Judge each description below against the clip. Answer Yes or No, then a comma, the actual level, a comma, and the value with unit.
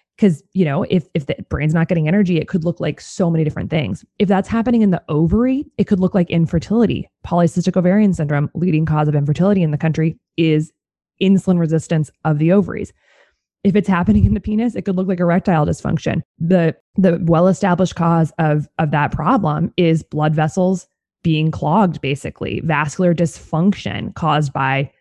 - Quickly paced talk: No, average, 180 wpm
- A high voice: No, medium, 170 Hz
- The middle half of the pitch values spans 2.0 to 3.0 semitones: No, average, 3.6 semitones